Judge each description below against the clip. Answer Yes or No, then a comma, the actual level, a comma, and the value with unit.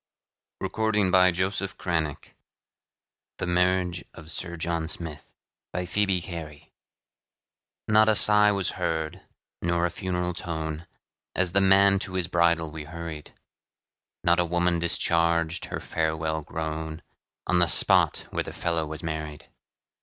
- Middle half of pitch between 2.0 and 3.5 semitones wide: Yes, narrow, 2.4 semitones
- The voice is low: Yes, very low, 85 Hz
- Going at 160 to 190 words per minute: No, average, 140 wpm